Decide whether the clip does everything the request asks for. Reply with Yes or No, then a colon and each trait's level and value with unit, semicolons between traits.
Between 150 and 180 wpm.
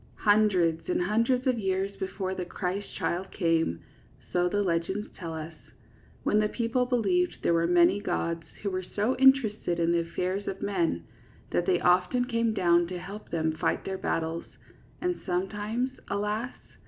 Yes: average, 170 wpm